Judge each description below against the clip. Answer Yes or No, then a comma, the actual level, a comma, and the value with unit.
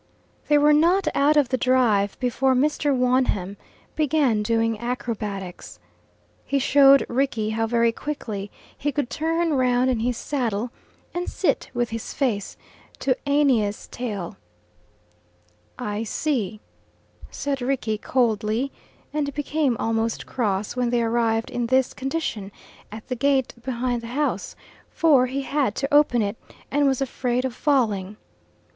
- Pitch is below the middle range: No, very high, 250 Hz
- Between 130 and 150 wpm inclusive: Yes, average, 140 wpm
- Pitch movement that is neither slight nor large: Yes, average, 3.7 semitones